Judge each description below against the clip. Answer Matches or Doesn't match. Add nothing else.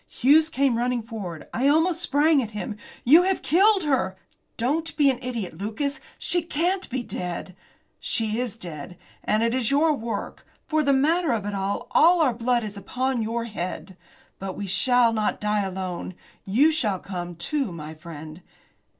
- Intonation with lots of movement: Matches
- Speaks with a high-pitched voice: Matches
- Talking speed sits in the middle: Matches